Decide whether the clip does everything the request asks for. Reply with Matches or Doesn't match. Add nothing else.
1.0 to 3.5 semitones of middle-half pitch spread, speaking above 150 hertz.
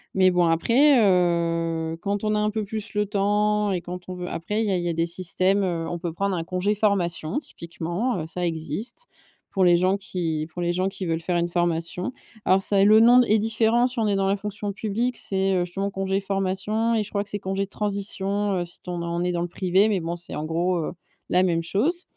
Matches